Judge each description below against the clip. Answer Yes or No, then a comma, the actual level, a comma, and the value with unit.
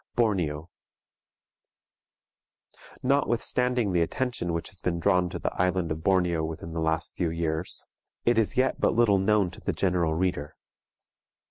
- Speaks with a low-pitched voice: Yes, very low, 90 Hz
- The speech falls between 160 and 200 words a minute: No, average, 145 wpm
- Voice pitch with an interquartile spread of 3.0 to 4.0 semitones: No, average, 4.5 semitones